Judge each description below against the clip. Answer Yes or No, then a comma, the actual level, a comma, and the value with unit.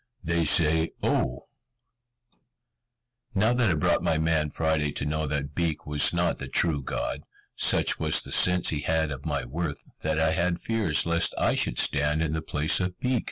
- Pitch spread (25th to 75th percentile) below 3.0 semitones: Yes, narrow, 2.5 semitones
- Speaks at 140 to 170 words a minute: No, average, 185 wpm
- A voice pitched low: Yes, very low, 80 Hz